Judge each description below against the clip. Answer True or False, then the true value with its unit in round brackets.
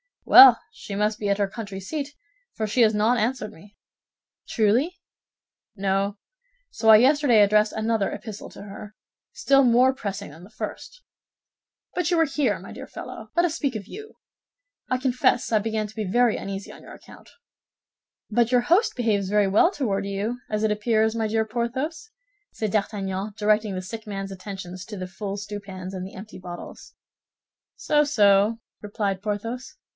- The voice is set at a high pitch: True (215 Hz)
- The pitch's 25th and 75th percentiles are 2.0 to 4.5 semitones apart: True (3.4 semitones)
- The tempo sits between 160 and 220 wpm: True (170 wpm)